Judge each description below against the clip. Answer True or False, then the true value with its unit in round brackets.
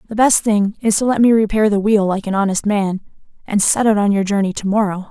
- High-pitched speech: True (205 Hz)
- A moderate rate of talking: False (260 wpm)